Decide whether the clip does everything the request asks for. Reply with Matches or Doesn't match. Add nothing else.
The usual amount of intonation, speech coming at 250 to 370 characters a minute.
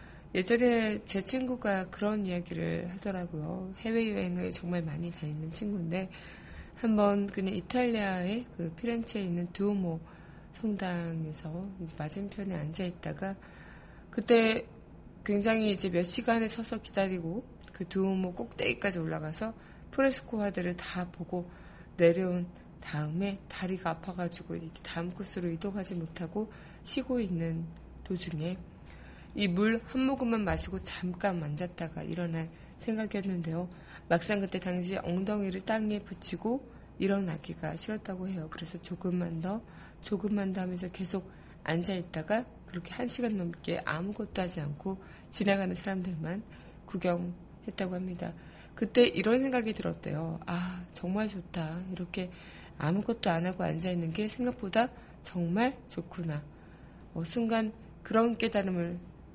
Matches